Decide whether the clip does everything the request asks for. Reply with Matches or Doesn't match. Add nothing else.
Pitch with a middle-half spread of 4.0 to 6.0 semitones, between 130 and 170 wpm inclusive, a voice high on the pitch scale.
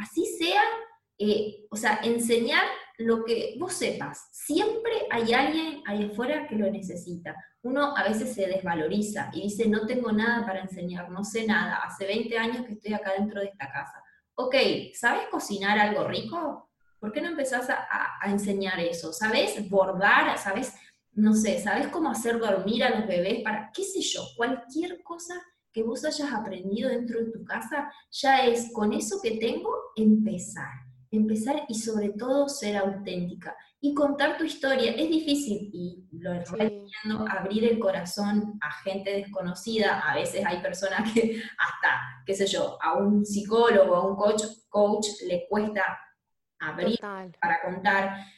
Matches